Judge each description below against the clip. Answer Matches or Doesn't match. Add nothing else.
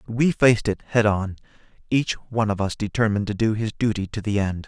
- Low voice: Matches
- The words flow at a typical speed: Doesn't match